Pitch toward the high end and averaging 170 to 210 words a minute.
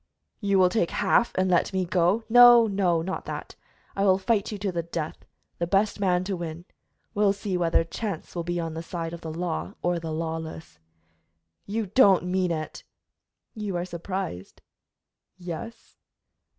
No: medium, 180 Hz; average, 175 wpm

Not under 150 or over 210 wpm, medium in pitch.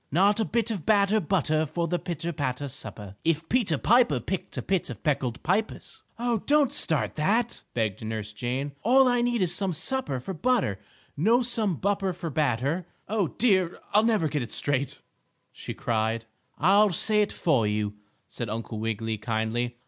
Yes: average, 180 wpm; medium, 165 Hz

